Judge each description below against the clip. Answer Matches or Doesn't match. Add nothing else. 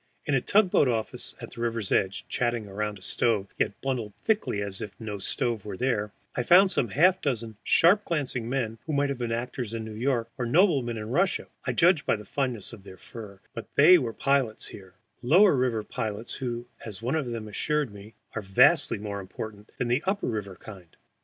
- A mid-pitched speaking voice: Doesn't match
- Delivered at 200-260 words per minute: Matches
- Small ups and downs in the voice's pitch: Doesn't match